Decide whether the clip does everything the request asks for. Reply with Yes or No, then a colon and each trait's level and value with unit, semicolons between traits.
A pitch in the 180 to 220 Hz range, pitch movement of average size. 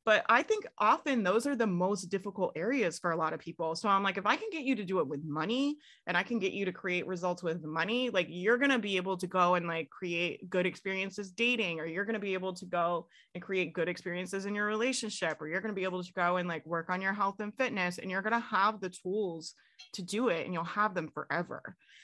Yes: medium, 185 Hz; average, 3.3 semitones